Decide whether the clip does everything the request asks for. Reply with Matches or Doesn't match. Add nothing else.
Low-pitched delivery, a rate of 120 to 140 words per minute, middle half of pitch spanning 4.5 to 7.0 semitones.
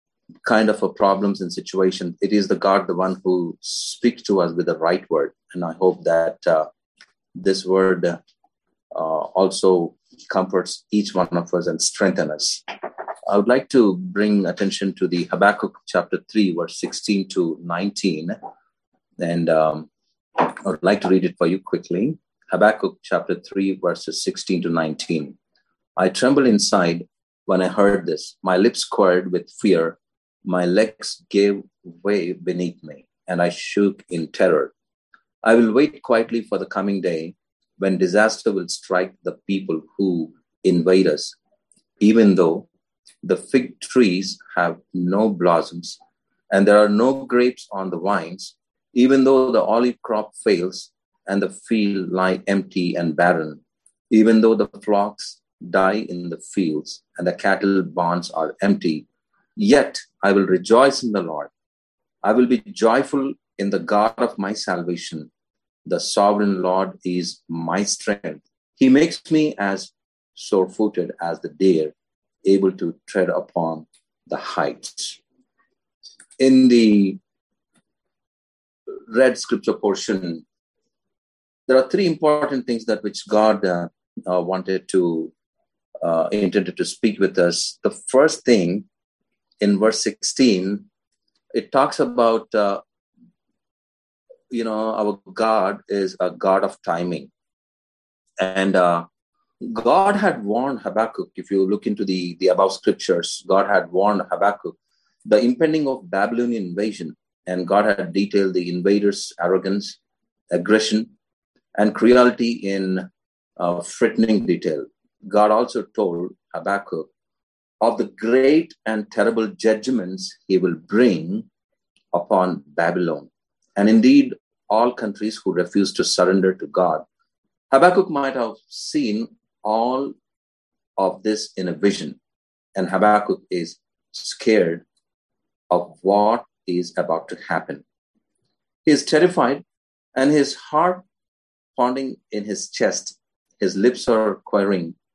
Doesn't match